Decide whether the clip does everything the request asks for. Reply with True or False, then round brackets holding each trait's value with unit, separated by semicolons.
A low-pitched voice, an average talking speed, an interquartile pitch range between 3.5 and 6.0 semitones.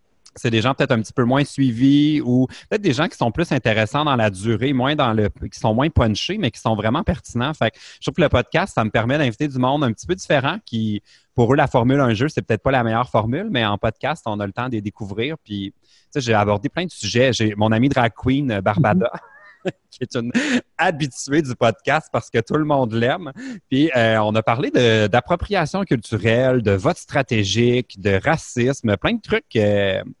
False (120 Hz; 225 wpm; 4.3 semitones)